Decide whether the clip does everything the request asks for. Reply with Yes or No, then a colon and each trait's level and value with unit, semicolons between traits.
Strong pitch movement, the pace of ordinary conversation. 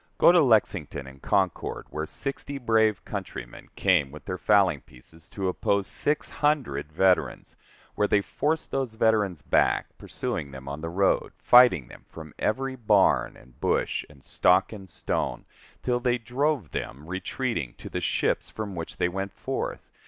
Yes: wide, 7.6 semitones; average, 160 wpm